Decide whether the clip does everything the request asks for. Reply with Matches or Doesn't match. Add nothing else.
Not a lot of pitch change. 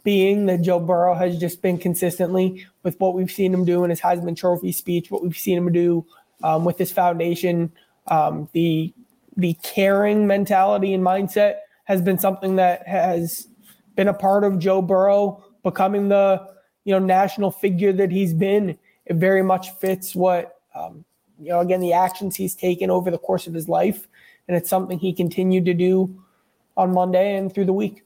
Matches